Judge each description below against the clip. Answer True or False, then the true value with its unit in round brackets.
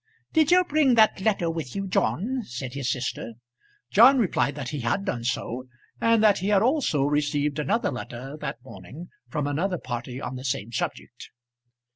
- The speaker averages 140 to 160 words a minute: False (175 wpm)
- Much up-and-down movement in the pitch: True (8.3 semitones)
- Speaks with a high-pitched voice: False (150 Hz)